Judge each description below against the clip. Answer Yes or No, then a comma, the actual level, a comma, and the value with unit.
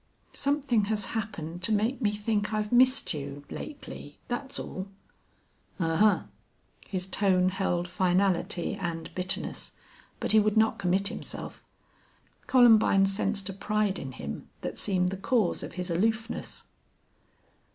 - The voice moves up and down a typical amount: Yes, average, 3.3 semitones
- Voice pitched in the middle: No, high, 200 Hz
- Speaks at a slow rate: Yes, slow, 130 wpm